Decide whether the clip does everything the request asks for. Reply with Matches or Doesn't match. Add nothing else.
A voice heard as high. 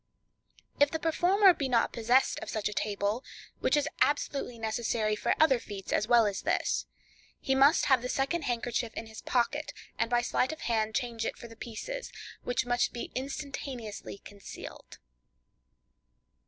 Matches